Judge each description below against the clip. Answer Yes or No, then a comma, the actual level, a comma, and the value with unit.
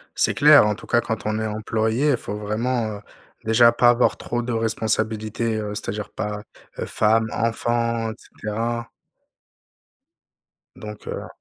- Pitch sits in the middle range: No, low, 110 Hz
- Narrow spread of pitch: Yes, narrow, 1.7 semitones